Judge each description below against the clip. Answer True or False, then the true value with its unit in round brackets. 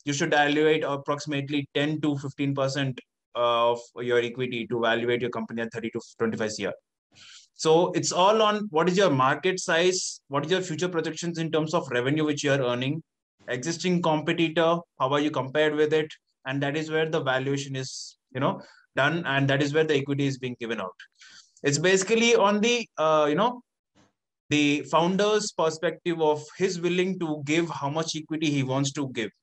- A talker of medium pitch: True (150 Hz)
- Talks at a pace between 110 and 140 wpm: False (190 wpm)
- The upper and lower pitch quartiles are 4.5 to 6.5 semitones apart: False (3.8 semitones)